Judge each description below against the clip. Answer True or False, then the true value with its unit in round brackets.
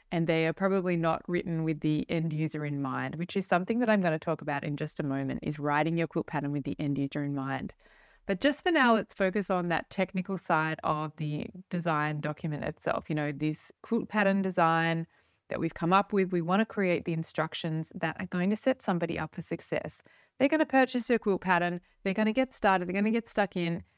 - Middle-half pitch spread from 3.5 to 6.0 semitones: True (3.8 semitones)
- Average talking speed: False (240 wpm)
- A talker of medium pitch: True (170 Hz)